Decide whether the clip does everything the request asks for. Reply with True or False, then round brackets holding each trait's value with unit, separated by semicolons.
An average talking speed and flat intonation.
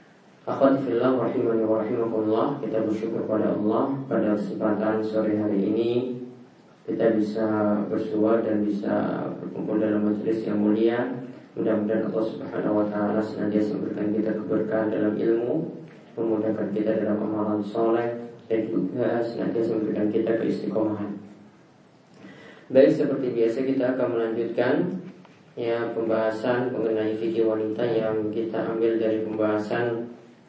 True (115 wpm; 1.4 semitones)